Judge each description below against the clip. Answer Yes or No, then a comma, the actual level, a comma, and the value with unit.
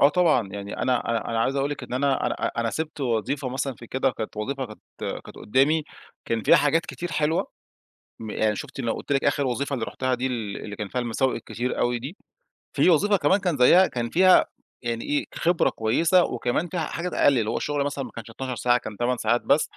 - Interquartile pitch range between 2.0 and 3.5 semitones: No, average, 4.0 semitones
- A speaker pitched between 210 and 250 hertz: No, low, 130 Hz